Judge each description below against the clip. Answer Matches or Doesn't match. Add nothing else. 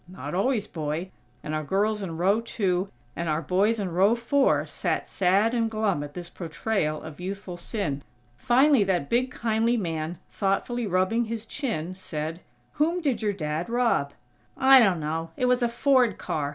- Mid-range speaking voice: Doesn't match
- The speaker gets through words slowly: Doesn't match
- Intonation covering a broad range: Matches